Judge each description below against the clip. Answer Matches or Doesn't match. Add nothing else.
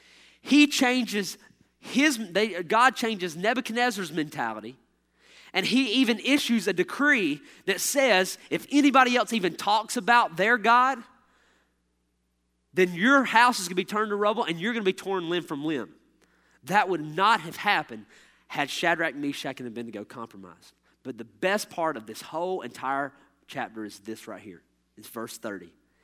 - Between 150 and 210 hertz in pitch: Matches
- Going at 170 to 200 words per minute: Doesn't match